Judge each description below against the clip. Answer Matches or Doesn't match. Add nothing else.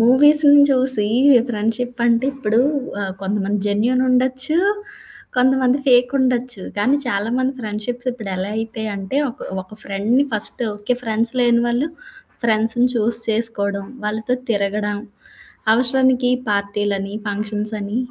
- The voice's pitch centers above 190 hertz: Matches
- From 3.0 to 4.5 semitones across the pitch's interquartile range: Matches